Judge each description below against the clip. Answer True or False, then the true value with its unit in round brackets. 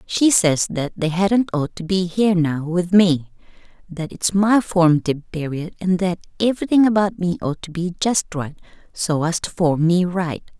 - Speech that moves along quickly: False (180 wpm)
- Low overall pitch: False (175 Hz)